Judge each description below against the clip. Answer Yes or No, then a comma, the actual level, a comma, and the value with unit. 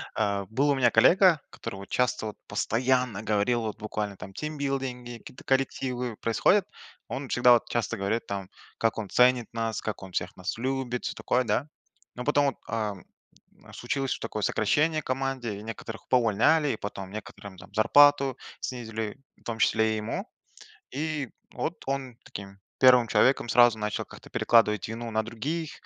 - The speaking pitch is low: Yes, low, 120 Hz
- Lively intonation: No, average, 3.6 semitones